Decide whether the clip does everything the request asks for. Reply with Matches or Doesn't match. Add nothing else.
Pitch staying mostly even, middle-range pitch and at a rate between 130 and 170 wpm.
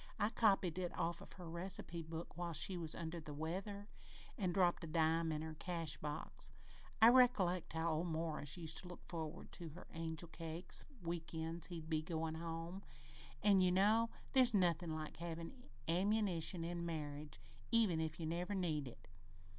Doesn't match